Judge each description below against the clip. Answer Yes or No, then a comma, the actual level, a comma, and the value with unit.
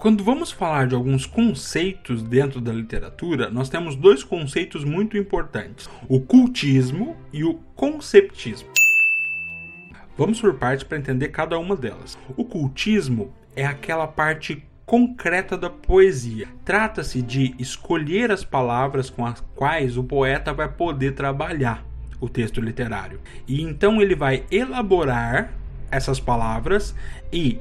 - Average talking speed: Yes, average, 130 wpm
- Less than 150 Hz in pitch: Yes, medium, 140 Hz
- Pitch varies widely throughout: Yes, wide, 6.8 semitones